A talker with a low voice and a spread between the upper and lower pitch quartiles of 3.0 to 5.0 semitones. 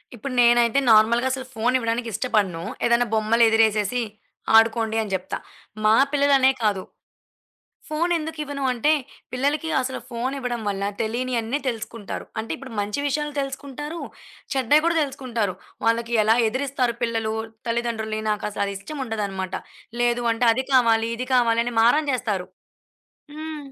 No: high, 235 Hz; average, 3.3 semitones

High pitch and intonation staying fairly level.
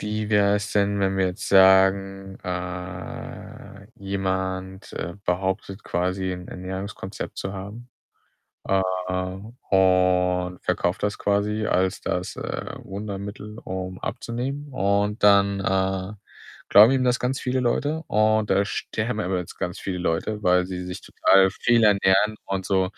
No: very low, 95 Hz; narrow, 2.0 semitones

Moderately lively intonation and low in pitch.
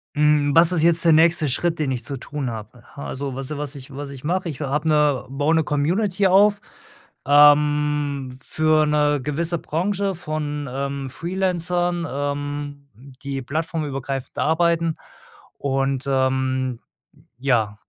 No: average, 3.1 semitones; medium, 145 Hz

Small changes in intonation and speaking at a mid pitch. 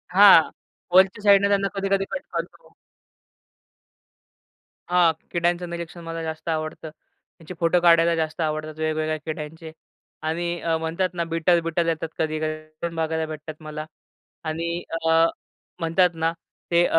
Yes: narrow, 1.7 semitones; medium, 165 Hz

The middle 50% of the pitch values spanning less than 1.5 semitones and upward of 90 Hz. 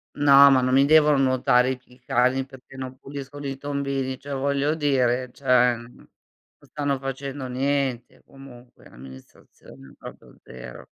No: narrow, 1.9 semitones; low, 135 Hz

